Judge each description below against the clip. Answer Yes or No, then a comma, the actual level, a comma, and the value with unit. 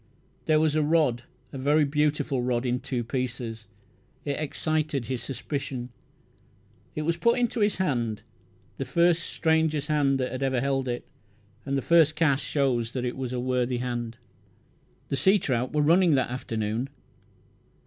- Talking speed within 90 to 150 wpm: No, average, 160 wpm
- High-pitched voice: No, low, 135 Hz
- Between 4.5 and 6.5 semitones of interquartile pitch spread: No, average, 3.7 semitones